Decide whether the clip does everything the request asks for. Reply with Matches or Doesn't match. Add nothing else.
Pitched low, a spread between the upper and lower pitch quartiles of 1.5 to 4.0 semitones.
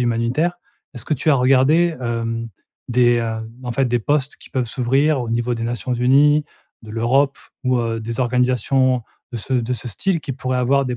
Matches